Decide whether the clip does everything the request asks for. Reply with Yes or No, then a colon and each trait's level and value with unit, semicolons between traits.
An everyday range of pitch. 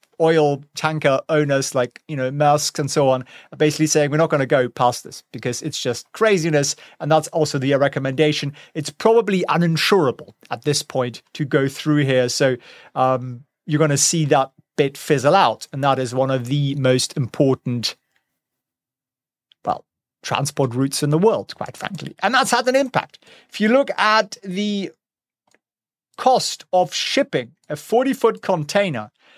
Yes: average, 4.7 semitones